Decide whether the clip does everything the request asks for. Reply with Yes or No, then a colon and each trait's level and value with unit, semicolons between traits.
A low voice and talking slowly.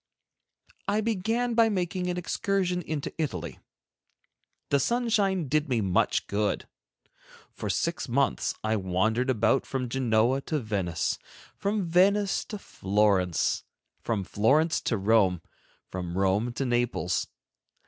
Yes: low, 130 Hz; slow, 125 wpm